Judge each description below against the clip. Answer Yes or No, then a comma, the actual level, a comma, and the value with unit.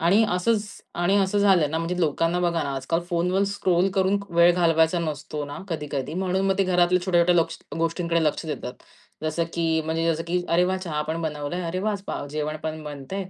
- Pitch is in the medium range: Yes, medium, 170 Hz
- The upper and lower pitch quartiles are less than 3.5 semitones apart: Yes, narrow, 2.6 semitones